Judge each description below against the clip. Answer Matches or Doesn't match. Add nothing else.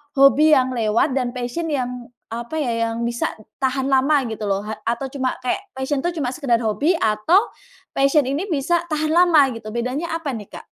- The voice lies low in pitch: Doesn't match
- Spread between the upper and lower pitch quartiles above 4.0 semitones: Matches